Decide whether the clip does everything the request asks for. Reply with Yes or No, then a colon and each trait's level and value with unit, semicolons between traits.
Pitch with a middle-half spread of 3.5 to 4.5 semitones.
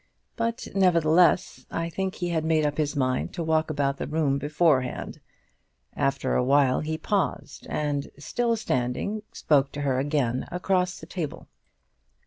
Yes: average, 4.0 semitones